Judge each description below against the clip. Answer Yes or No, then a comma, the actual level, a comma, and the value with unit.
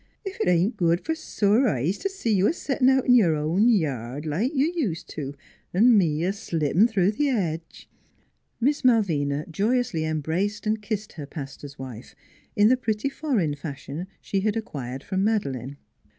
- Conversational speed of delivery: Yes, average, 180 wpm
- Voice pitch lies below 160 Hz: No, high, 190 Hz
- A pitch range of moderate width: No, wide, 7.0 semitones